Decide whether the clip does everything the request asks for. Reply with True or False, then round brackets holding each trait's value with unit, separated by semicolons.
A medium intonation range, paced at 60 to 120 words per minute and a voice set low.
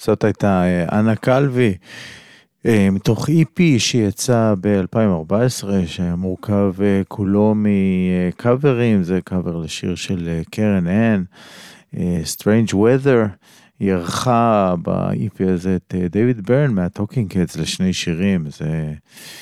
True (4.0 semitones; 100 wpm; 100 Hz)